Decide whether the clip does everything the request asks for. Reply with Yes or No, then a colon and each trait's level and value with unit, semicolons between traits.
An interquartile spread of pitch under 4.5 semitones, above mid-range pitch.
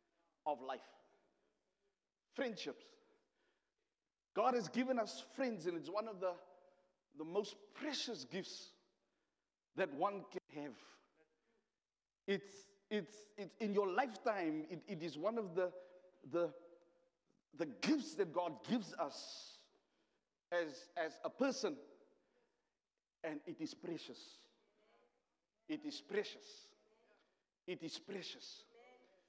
No: average, 5.1 semitones; high, 205 Hz